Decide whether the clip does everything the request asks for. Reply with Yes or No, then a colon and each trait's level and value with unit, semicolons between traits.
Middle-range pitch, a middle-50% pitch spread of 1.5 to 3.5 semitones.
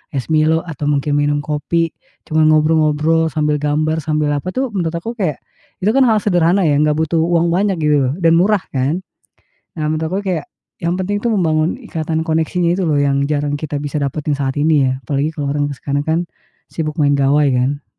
Yes: medium, 155 Hz; narrow, 2.6 semitones